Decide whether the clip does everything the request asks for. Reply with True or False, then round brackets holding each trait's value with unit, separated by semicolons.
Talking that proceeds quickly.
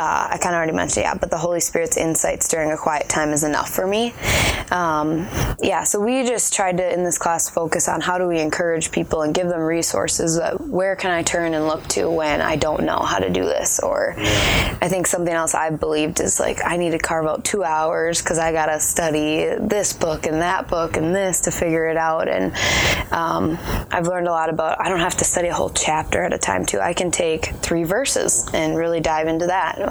True (240 wpm)